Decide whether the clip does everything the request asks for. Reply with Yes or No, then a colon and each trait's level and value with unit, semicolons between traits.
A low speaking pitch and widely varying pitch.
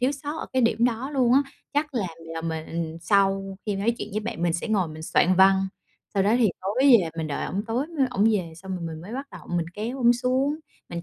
No: high, 200 Hz; wide, 6.4 semitones